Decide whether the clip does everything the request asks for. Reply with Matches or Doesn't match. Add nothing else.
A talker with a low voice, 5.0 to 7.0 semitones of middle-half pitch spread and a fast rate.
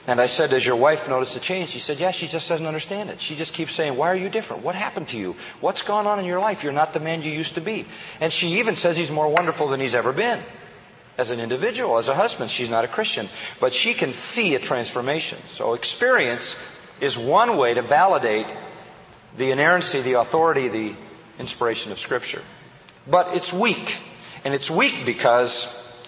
Doesn't match